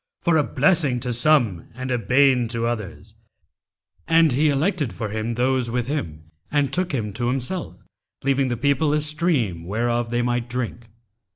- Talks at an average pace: Yes, average, 170 wpm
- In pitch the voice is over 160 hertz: No, low, 125 Hz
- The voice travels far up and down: No, average, 3.7 semitones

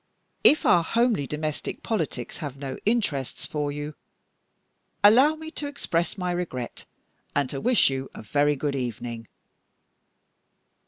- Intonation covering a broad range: Yes, wide, 7.5 semitones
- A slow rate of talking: Yes, slow, 130 wpm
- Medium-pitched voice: Yes, medium, 150 Hz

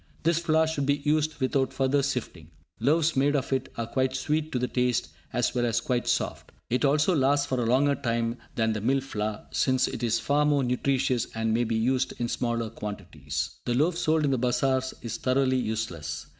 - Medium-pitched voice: No, low, 130 Hz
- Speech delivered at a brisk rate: Yes, fast, 210 wpm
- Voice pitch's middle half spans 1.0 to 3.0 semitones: No, average, 3.5 semitones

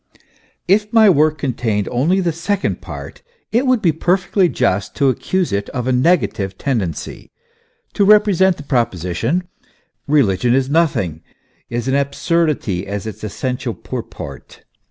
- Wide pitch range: Yes, wide, 8.6 semitones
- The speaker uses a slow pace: No, average, 145 wpm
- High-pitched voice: No, medium, 140 Hz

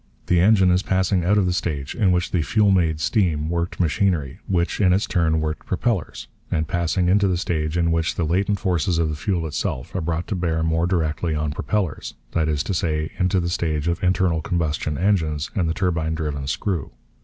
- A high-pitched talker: No, very low, 85 Hz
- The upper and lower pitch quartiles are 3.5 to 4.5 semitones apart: No, average, 2.9 semitones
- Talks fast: Yes, fast, 210 wpm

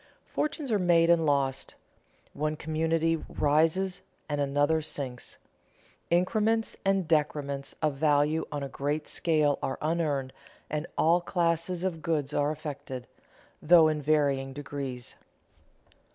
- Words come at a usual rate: No, slow, 125 wpm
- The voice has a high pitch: No, medium, 155 Hz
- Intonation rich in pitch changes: No, average, 2.7 semitones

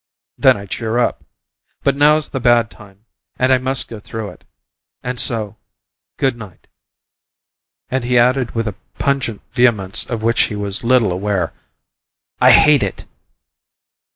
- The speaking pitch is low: Yes, low, 115 Hz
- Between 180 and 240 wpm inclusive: No, average, 150 wpm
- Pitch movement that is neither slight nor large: Yes, average, 3.5 semitones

